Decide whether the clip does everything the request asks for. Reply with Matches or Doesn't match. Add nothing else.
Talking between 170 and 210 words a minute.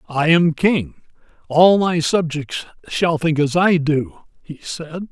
Doesn't match